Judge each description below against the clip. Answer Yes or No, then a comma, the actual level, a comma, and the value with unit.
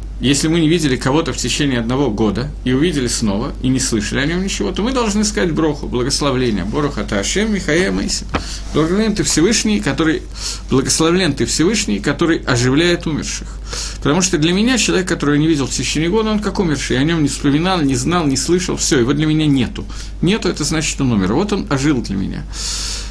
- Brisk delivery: Yes, fast, 205 wpm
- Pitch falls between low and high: Yes, medium, 150 Hz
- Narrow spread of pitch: No, average, 5.3 semitones